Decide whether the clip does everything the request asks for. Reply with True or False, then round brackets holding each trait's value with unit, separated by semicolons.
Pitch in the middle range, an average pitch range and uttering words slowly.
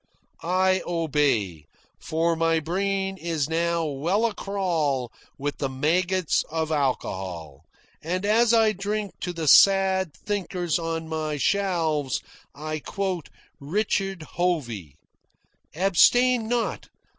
True (170 Hz; 4.5 semitones; 110 wpm)